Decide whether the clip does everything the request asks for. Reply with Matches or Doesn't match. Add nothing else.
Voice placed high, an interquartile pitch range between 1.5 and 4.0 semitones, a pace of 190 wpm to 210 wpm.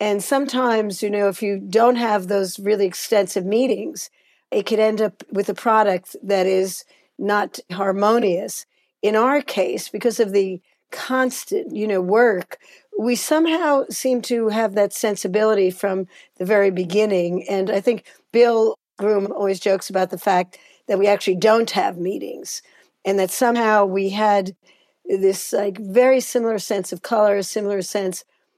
Doesn't match